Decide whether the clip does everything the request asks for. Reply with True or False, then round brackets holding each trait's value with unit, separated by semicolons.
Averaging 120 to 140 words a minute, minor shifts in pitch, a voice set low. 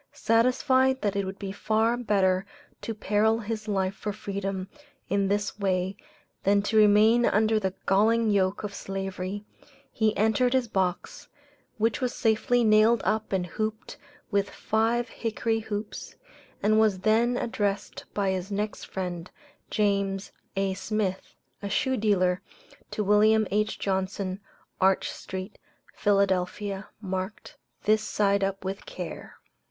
False (135 wpm; 2.2 semitones; 205 Hz)